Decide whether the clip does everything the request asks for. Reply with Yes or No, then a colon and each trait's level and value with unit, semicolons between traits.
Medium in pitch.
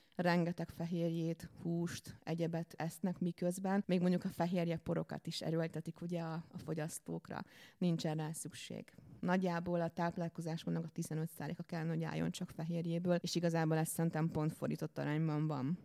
Yes: medium, 165 Hz